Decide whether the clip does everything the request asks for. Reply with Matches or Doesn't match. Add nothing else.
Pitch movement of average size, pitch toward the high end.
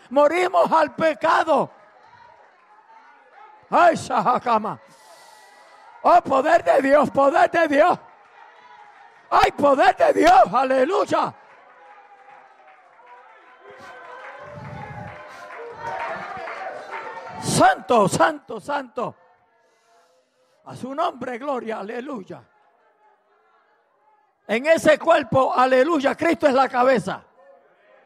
Doesn't match